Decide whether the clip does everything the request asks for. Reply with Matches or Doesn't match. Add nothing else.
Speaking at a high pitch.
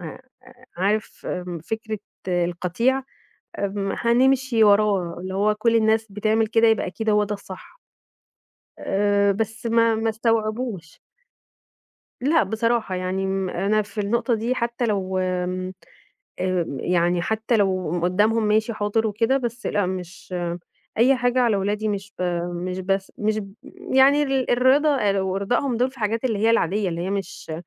Matches